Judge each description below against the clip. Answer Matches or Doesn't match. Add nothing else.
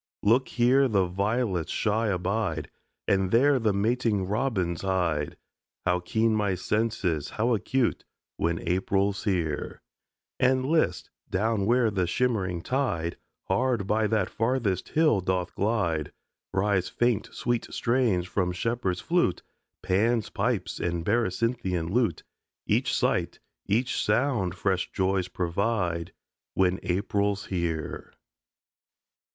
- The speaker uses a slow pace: Matches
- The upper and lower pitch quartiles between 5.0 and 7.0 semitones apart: Doesn't match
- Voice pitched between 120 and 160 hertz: Doesn't match